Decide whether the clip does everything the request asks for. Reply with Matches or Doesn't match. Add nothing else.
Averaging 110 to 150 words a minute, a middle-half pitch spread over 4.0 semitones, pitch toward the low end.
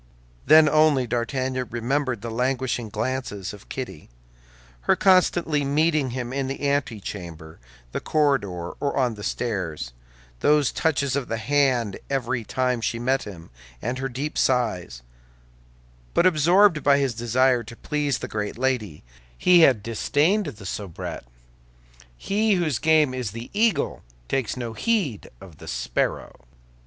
Matches